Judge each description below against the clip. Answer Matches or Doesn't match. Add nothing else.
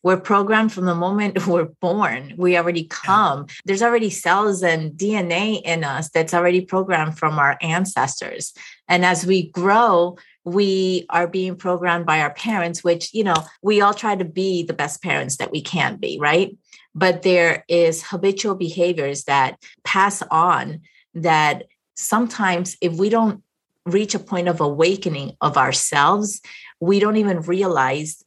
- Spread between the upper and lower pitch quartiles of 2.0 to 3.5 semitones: Matches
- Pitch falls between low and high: Matches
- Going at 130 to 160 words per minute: Matches